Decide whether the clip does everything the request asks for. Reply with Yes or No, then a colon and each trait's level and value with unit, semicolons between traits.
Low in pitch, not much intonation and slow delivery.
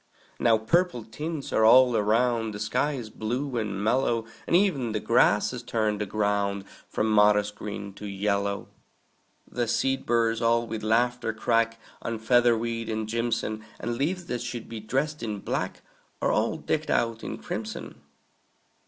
No: low, 115 Hz; narrow, 2.2 semitones; average, 155 wpm